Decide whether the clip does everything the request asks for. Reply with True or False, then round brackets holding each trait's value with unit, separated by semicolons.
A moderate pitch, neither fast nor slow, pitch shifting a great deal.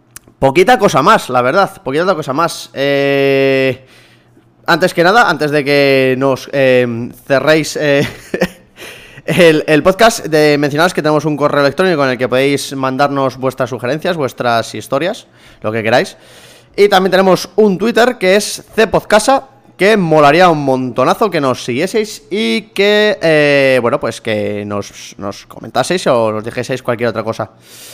True (145 Hz; 150 wpm; 5.9 semitones)